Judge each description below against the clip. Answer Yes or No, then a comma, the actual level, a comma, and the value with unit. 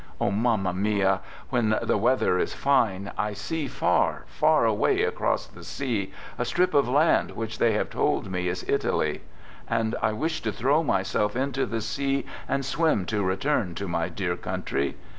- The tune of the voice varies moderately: No, wide, 5.8 semitones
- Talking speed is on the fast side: No, average, 175 wpm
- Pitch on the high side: No, low, 110 Hz